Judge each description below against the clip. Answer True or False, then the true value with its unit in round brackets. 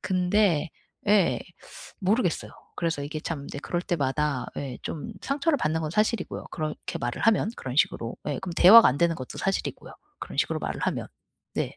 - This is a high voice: False (170 Hz)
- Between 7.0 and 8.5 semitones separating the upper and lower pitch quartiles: False (5.5 semitones)